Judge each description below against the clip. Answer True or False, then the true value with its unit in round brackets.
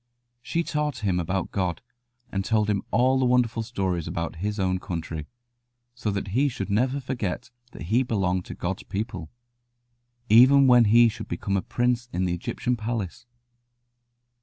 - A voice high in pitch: False (110 Hz)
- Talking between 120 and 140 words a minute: False (160 wpm)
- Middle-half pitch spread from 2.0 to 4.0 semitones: False (4.8 semitones)